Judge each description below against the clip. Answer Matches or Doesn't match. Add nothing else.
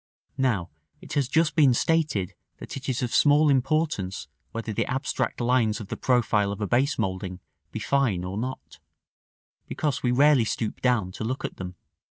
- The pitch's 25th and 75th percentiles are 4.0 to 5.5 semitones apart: Matches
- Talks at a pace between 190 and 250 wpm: Doesn't match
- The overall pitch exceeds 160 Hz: Doesn't match